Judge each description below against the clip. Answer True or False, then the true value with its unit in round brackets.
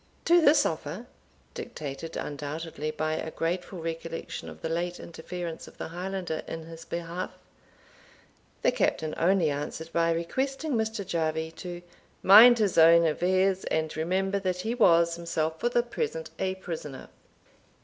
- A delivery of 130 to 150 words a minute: True (145 wpm)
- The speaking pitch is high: False (170 Hz)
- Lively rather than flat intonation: False (3.1 semitones)